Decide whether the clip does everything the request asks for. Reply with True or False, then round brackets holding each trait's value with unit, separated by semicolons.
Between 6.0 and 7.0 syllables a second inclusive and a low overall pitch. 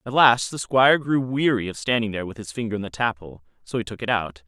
True (6.5 syllables/s; 110 Hz)